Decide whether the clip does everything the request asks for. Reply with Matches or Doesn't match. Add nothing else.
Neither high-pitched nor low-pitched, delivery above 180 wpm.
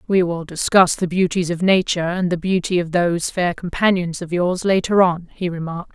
Matches